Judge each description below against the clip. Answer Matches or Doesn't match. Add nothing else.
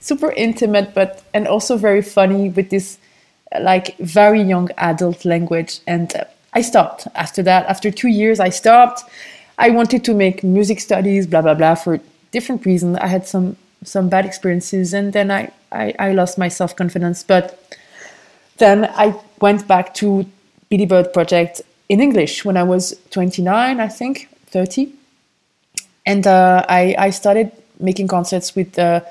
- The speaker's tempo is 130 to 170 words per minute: Matches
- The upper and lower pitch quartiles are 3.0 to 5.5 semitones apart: Doesn't match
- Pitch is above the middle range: Matches